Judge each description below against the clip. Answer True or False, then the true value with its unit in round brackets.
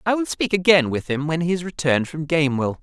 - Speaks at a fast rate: True (255 wpm)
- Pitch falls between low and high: True (160 Hz)